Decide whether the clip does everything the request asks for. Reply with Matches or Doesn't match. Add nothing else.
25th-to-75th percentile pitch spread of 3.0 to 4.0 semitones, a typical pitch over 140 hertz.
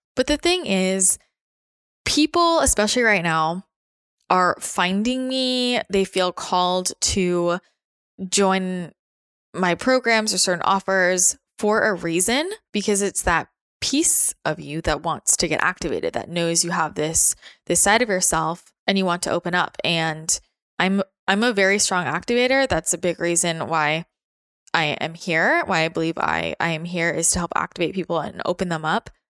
Matches